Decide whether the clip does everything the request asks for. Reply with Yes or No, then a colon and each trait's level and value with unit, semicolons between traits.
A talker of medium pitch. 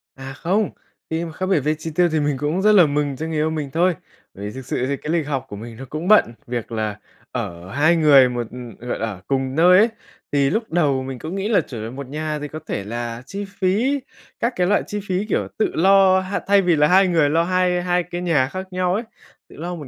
Yes: medium, 155 Hz